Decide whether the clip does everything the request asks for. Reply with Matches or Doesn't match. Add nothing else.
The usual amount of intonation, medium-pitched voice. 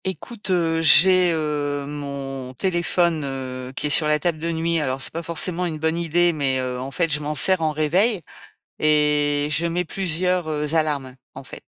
Matches